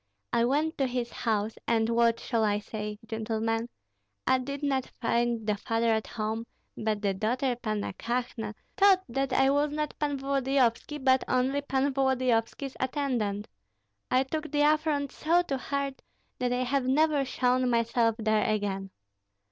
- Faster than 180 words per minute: No, average, 155 wpm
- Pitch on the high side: Yes, very high, 250 Hz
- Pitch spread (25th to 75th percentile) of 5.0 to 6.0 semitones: No, average, 3.5 semitones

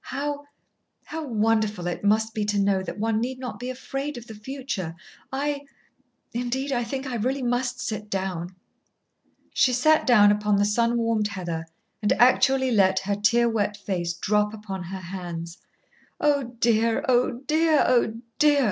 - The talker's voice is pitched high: Yes, high, 225 Hz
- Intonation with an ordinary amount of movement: Yes, average, 4.1 semitones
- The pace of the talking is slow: No, average, 165 wpm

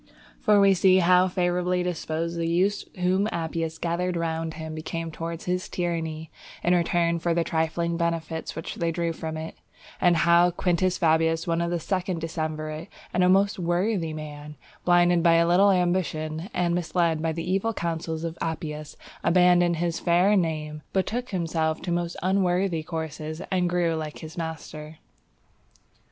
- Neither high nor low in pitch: Yes, medium, 170 Hz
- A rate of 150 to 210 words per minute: Yes, average, 160 wpm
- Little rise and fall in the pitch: Yes, narrow, 1.8 semitones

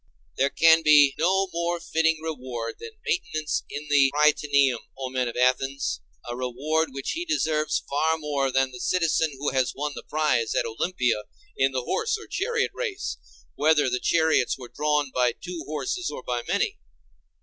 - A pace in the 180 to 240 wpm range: No, average, 170 wpm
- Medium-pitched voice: Yes, medium, 150 Hz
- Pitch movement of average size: Yes, average, 3.8 semitones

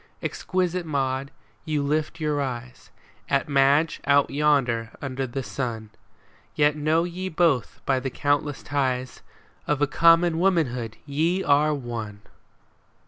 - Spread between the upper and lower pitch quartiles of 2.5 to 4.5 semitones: Yes, average, 3.2 semitones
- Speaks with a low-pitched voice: No, medium, 145 Hz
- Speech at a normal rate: No, slow, 130 wpm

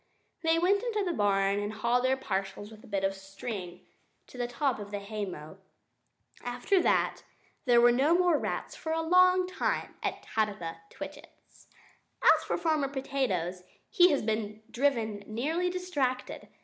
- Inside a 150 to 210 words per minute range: Yes, average, 160 wpm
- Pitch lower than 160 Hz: No, high, 240 Hz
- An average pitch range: No, wide, 7.8 semitones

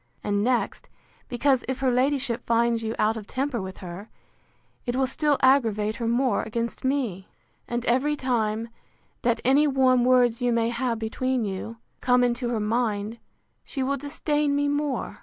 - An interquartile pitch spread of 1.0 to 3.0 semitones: Yes, narrow, 2.6 semitones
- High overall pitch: Yes, high, 245 Hz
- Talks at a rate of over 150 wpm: Yes, average, 165 wpm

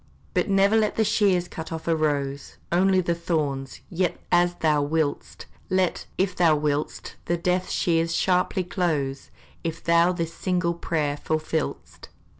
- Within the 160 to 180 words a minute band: No, average, 150 wpm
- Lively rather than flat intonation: No, narrow, 2.6 semitones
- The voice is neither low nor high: Yes, medium, 170 Hz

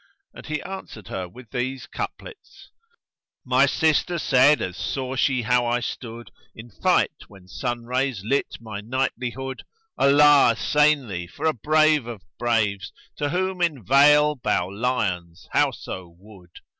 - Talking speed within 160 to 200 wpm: No, average, 150 wpm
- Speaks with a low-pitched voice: Yes, low, 125 Hz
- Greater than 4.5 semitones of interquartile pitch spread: Yes, average, 5.2 semitones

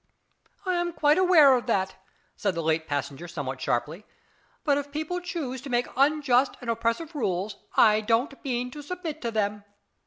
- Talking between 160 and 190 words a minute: Yes, average, 175 wpm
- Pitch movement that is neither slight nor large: No, wide, 6.9 semitones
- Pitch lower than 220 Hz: No, high, 245 Hz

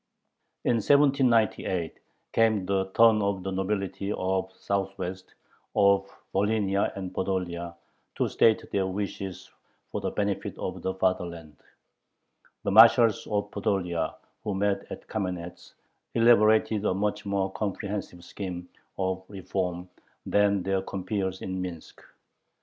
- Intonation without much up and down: Yes, narrow, 1.9 semitones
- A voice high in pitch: No, very low, 95 Hz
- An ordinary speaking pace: No, slow, 120 wpm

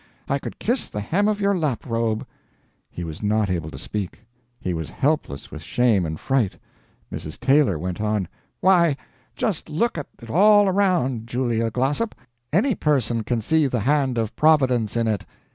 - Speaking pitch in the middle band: No, low, 125 Hz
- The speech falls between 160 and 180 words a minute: Yes, average, 170 wpm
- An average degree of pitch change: No, wide, 6.8 semitones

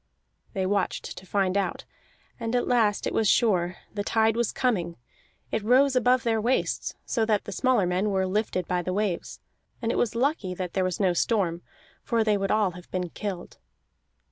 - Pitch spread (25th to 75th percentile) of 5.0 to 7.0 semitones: No, average, 3.8 semitones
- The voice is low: No, high, 205 Hz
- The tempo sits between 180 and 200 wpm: Yes, average, 195 wpm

